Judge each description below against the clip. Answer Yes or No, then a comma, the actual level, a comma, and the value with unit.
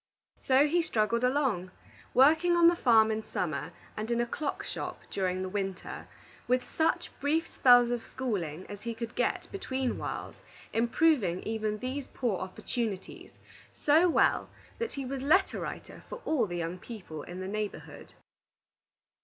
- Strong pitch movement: Yes, wide, 6.1 semitones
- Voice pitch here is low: No, high, 235 Hz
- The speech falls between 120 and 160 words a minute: Yes, average, 155 wpm